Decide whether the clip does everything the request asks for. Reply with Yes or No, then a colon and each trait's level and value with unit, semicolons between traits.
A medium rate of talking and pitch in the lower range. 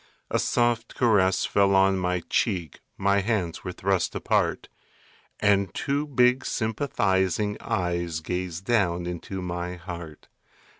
No: slow, 120 wpm; very low, 95 Hz